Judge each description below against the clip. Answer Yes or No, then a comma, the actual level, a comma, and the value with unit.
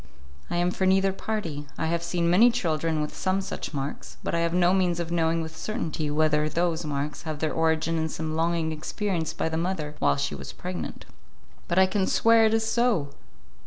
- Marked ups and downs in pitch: No, average, 3.1 semitones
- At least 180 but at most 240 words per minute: Yes, fast, 205 wpm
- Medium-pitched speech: Yes, medium, 165 Hz